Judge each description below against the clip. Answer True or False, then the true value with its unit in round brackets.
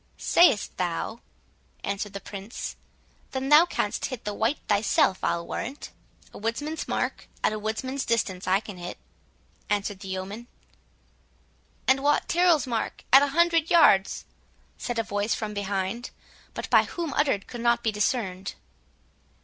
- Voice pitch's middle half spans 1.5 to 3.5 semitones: False (5.3 semitones)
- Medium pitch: False (225 Hz)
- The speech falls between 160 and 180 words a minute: False (150 wpm)